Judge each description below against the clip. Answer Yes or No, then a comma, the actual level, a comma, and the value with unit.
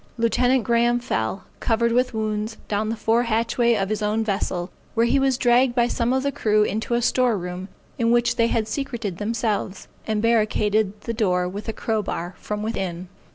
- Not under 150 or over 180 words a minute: No, average, 195 wpm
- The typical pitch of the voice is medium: No, high, 225 Hz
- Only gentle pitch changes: Yes, narrow, 2.3 semitones